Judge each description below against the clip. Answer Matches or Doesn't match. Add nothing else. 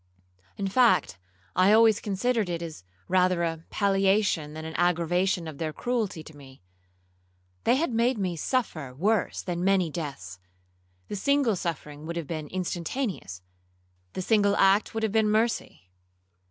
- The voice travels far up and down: Matches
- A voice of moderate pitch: Matches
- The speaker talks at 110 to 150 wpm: Matches